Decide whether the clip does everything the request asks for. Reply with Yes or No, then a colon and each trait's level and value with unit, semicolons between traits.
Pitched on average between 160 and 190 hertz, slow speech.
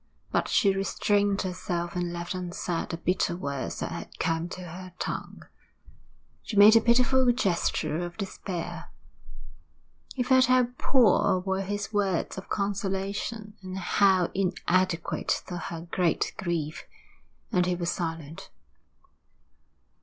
Yes: medium, 185 Hz; slow, 130 wpm